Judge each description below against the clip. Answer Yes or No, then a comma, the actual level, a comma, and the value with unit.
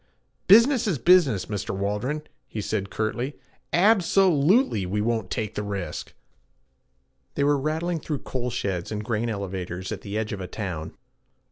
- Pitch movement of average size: No, wide, 7.4 semitones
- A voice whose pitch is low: Yes, low, 110 Hz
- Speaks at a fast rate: No, average, 165 wpm